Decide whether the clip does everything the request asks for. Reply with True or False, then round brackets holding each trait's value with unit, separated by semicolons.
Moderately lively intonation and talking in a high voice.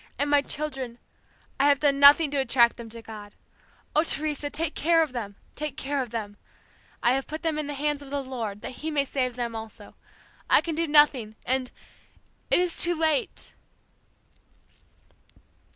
True (3.8 semitones; 280 Hz)